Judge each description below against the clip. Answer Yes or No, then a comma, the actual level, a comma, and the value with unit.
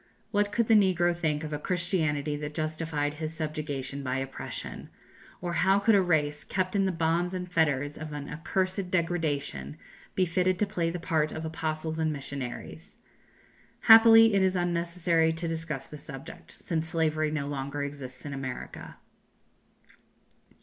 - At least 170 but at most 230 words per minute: No, average, 155 wpm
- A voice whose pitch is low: No, medium, 160 Hz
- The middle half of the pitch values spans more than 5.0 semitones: No, average, 3.3 semitones